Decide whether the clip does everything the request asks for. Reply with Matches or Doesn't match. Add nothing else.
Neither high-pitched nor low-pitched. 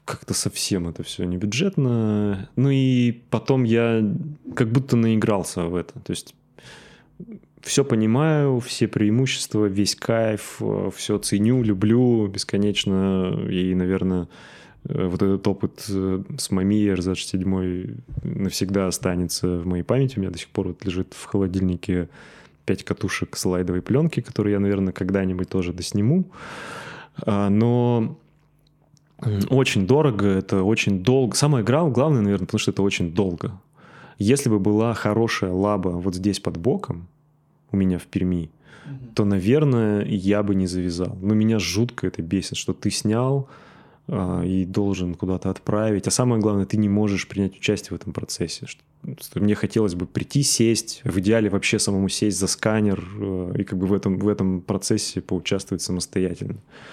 Doesn't match